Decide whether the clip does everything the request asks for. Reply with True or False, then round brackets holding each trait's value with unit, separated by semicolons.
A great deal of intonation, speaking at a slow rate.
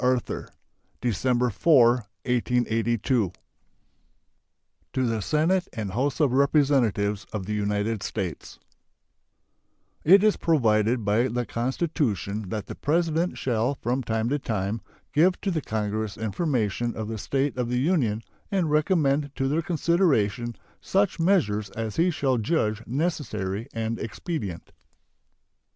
True (5.7 semitones; 125 wpm)